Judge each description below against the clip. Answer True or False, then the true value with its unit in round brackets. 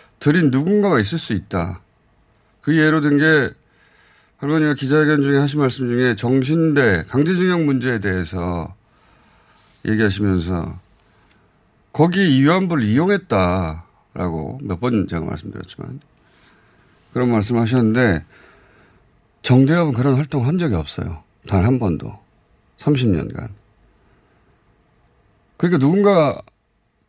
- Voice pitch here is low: True (125 Hz)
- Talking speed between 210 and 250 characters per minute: True (245 characters per minute)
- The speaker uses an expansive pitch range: True (7.1 semitones)